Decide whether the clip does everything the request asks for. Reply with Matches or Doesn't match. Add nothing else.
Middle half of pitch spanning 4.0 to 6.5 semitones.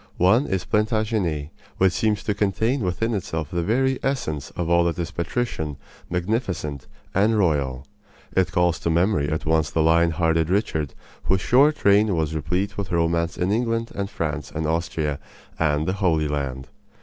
Matches